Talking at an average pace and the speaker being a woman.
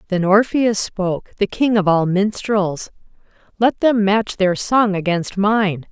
Yes: average, 150 wpm; female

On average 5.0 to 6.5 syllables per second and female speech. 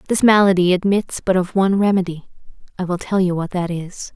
Yes: 5.9 syllables/s; female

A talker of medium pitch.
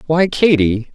Yes: medium, 150 Hz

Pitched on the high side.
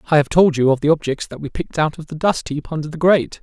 No: medium, 155 Hz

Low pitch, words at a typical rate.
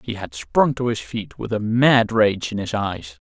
No: low, 110 Hz; fast, 240 wpm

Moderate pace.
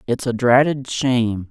Yes: average, 160 wpm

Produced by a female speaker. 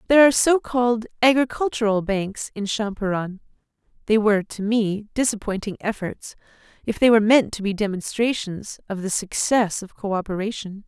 Yes: female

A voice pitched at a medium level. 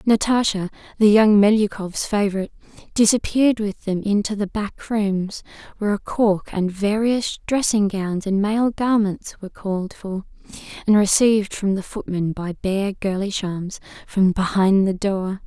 No: high, 200 Hz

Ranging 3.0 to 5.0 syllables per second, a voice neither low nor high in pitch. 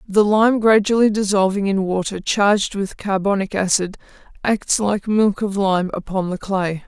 No: 4.5 syllables/s; high, 200 Hz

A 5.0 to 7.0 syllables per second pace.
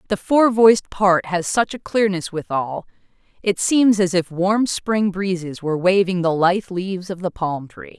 No: 4.6 syllables/s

